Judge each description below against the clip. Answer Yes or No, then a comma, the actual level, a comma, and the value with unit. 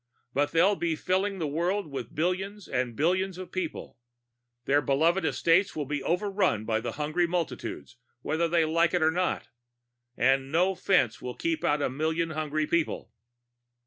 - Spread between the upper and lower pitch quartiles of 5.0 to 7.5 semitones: No, average, 4.0 semitones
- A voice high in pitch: No, medium, 165 Hz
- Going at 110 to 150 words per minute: No, average, 165 wpm